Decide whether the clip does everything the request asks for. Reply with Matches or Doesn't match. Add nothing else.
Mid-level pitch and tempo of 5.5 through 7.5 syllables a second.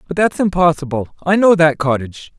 Matches